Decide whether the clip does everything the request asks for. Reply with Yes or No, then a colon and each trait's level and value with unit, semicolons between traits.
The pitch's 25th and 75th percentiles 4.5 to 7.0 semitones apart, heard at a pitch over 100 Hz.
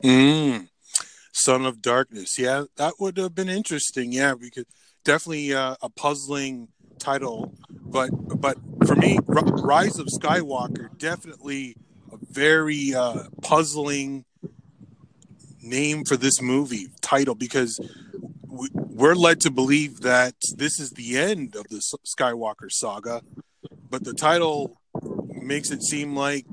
No: average, 3.0 semitones; medium, 140 Hz